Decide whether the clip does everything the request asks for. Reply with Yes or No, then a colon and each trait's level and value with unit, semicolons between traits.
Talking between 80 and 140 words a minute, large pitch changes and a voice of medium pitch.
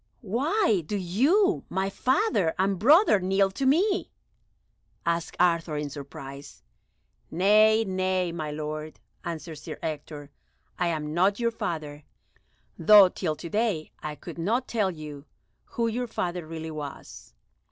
Yes: slow, 135 wpm; wide, 5.8 semitones; medium, 180 Hz